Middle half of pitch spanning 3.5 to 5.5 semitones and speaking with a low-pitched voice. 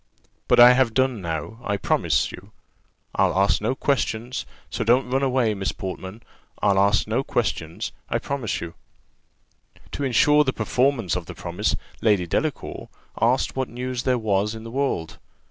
Yes: average, 4.6 semitones; low, 115 Hz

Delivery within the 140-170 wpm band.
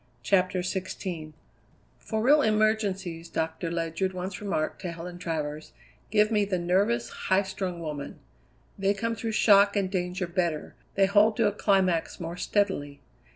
Yes: average, 150 wpm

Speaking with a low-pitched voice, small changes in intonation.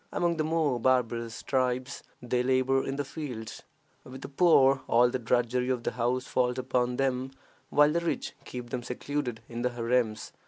Yes: low, 125 Hz; narrow, 1.8 semitones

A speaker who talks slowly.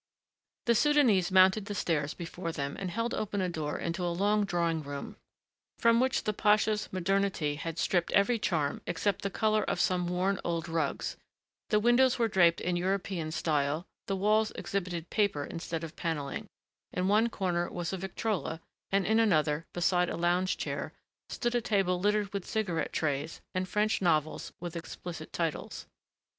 No: average, 170 wpm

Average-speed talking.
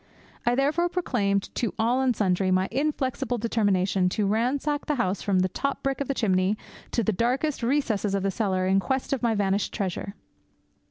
Yes: average, 185 wpm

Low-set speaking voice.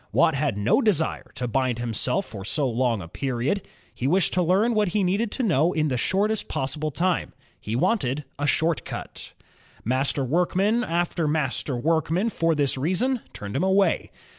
No: medium, 155 Hz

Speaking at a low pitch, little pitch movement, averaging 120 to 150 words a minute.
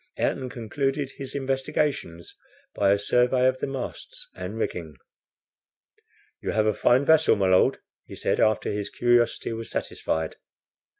No: low, 120 Hz; average, 4.7 semitones; average, 140 wpm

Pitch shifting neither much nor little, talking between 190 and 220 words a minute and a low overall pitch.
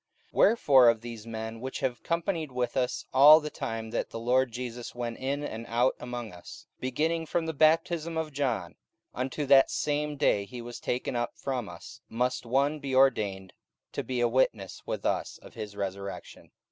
Yes: average, 3.7 semitones; average, 195 wpm; low, 125 Hz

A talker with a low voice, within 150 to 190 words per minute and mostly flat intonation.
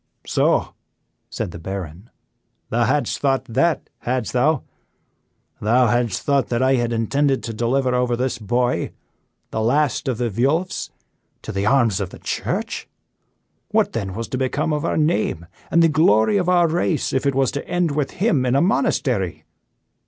No: low, 130 Hz; average, 170 wpm; average, 4.2 semitones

